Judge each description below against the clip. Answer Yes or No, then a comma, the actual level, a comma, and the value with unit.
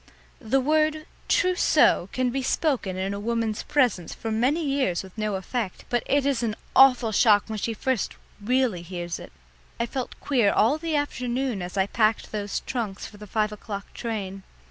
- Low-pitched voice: No, high, 230 Hz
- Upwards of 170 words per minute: Yes, average, 180 wpm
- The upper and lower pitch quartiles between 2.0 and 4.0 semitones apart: No, average, 4.6 semitones